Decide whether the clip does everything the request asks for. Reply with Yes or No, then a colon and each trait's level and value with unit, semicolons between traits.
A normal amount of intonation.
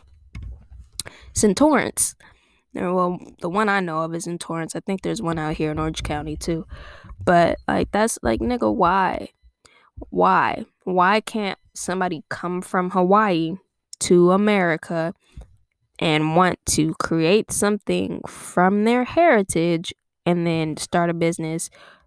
Yes: average, 3.2 semitones